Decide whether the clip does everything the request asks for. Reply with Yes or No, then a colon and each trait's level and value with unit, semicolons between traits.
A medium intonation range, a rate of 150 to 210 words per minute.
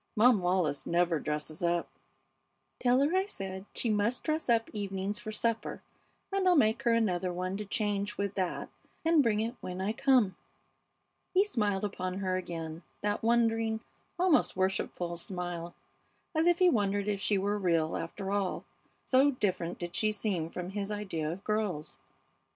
Yes: average, 4.0 semitones; average, 165 wpm